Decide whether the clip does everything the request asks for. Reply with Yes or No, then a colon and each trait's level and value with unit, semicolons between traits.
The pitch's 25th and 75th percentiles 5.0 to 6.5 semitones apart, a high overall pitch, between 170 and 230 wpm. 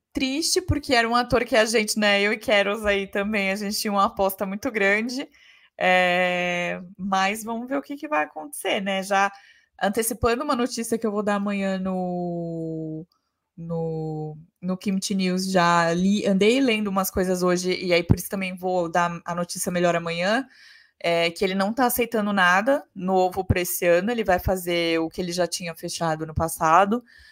No: average, 3.6 semitones; high, 195 Hz; fast, 185 wpm